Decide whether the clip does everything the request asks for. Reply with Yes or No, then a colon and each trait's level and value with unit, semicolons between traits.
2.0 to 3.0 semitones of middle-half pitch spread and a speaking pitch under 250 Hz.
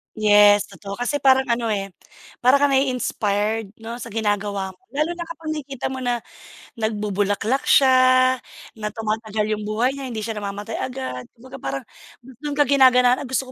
No: average, 4.0 semitones; high, 235 Hz